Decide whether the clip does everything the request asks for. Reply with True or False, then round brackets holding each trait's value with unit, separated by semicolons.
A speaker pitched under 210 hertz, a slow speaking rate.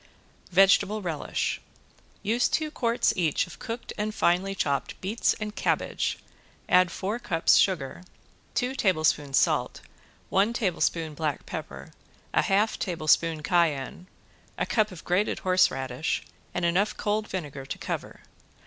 True (185 Hz; 130 wpm)